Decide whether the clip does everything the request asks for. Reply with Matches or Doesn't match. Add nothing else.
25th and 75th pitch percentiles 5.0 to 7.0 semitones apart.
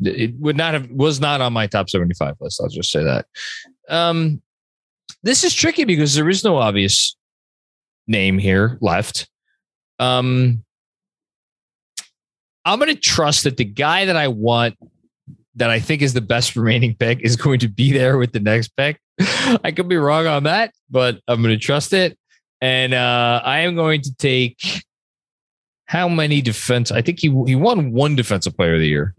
Matches